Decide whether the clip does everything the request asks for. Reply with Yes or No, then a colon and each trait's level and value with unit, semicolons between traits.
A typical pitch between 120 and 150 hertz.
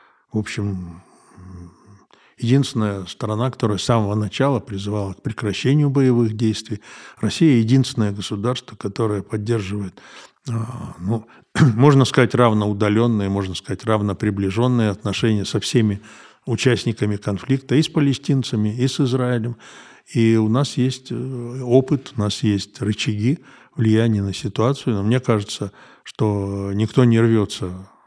No: low, 110 Hz